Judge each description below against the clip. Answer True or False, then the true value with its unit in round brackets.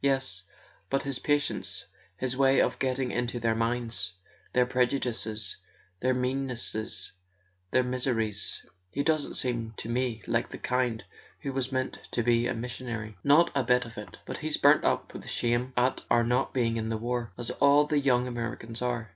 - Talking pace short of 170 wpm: False (175 wpm)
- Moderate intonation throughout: False (2.1 semitones)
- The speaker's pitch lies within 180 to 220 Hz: False (125 Hz)